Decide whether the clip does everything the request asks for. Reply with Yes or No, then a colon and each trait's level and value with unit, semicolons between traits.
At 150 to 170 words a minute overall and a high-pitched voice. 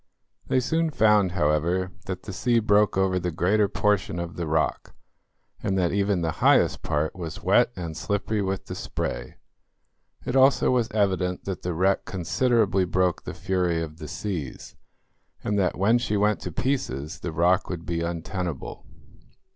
No: average, 165 wpm; very low, 95 Hz